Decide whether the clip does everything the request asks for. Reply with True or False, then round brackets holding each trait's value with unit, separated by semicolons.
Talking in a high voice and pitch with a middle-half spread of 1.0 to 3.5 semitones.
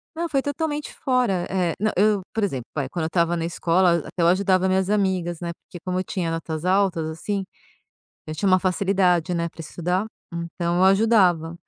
False (180 Hz; 2.7 semitones)